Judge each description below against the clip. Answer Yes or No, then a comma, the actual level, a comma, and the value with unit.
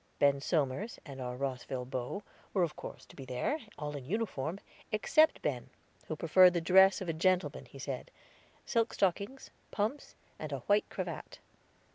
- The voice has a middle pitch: Yes, medium, 165 Hz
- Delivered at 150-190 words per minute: Yes, average, 165 wpm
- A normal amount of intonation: No, wide, 6.6 semitones